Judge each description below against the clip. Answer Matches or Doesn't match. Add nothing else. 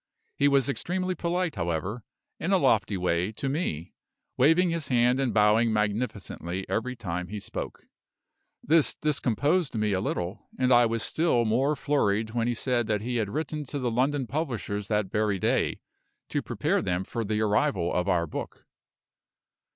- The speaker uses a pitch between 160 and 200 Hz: Doesn't match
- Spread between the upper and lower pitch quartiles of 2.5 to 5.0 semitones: Doesn't match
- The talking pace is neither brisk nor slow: Matches